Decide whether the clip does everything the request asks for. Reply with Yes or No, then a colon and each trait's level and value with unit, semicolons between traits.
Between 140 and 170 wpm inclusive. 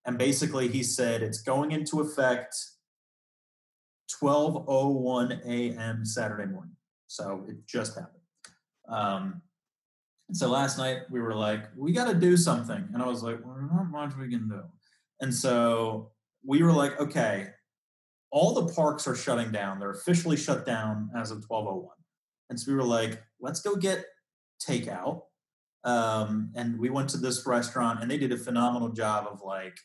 Yes: average, 165 wpm